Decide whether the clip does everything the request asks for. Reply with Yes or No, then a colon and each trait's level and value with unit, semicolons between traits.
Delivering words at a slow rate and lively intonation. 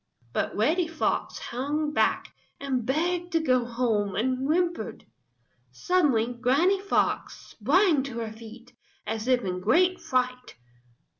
Yes: slow, 130 wpm; wide, 6.0 semitones